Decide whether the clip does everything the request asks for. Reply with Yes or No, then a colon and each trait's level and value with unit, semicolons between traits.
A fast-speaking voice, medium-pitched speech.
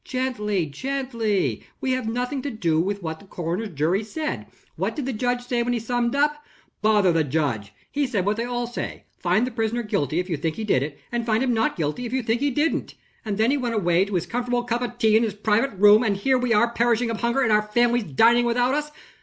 No: fast, 245 wpm; high, 225 Hz